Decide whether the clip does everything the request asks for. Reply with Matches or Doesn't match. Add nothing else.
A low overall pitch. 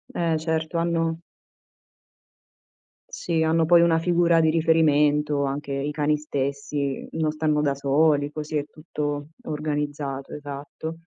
Doesn't match